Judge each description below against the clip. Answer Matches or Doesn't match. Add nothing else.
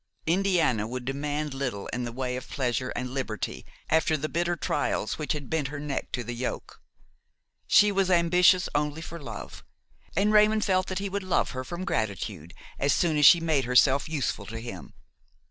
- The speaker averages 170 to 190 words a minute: Matches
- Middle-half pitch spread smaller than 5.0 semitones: Doesn't match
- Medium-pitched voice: Matches